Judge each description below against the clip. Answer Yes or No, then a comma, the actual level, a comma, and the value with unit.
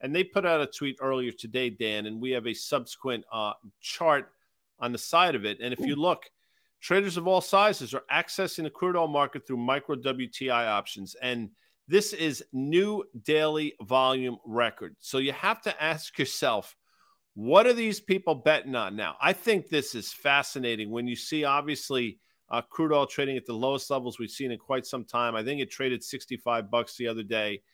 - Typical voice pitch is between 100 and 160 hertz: Yes, low, 135 Hz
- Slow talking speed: No, average, 195 wpm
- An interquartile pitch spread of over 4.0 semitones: Yes, average, 4.7 semitones